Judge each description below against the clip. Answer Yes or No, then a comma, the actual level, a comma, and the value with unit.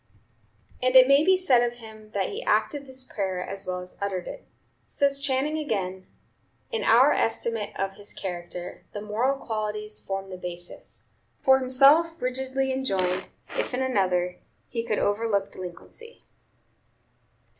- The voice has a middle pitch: No, high, 220 Hz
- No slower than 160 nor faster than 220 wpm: No, average, 145 wpm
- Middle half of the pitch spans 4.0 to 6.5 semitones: Yes, wide, 5.5 semitones